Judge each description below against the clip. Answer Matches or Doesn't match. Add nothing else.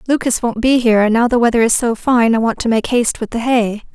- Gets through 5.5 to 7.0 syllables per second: Matches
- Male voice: Doesn't match